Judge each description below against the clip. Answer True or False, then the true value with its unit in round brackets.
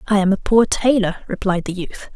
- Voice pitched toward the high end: True (200 Hz)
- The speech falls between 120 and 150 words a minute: False (225 wpm)